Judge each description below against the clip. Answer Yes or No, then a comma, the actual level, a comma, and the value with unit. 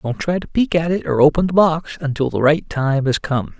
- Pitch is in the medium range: Yes, medium, 155 Hz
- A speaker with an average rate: No, fast, 265 wpm